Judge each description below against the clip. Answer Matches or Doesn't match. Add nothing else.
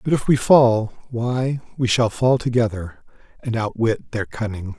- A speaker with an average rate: Matches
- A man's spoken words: Matches